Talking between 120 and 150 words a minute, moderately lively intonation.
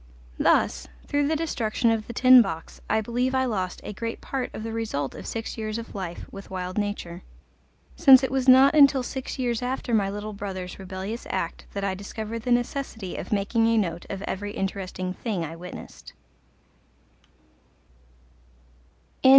No: average, 165 wpm; average, 4.5 semitones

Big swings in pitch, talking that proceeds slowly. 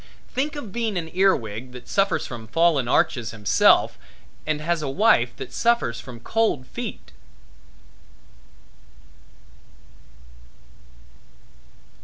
Yes: wide, 8.7 semitones; slow, 105 wpm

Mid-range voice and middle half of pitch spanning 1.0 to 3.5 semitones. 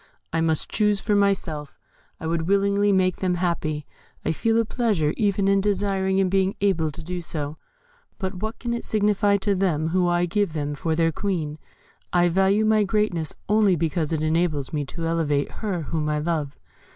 No: medium, 180 Hz; average, 4.0 semitones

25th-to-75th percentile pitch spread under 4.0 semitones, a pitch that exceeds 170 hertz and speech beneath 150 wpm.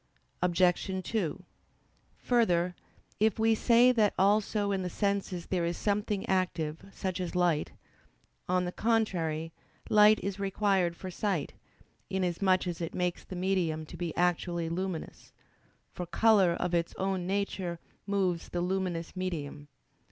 Yes: narrow, 2.6 semitones; medium, 185 Hz; slow, 135 wpm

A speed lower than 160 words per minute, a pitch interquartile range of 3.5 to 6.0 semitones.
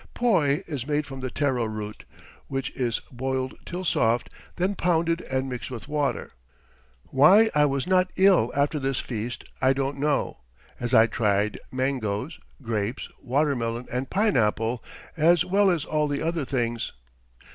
Yes: average, 150 wpm; average, 4.4 semitones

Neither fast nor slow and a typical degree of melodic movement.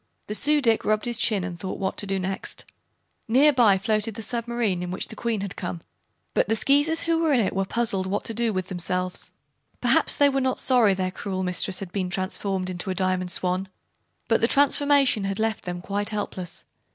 No: fast, 210 wpm; average, 4.2 semitones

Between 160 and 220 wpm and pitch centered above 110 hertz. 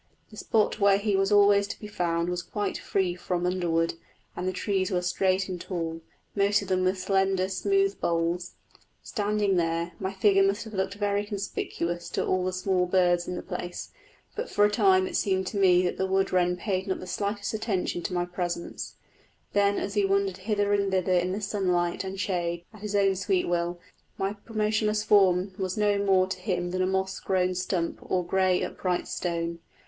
Yes: average, 195 wpm; high, 190 Hz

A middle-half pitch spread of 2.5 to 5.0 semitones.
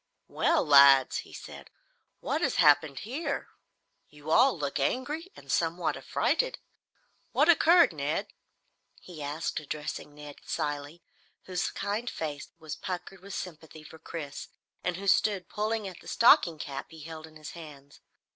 No: wide, 5.4 semitones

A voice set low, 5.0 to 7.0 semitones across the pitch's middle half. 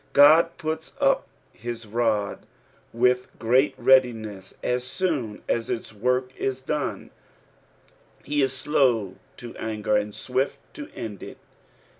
No: low, 125 Hz; average, 3.3 semitones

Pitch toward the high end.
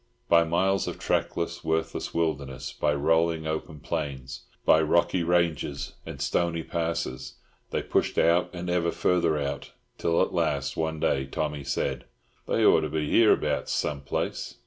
No: very low, 80 Hz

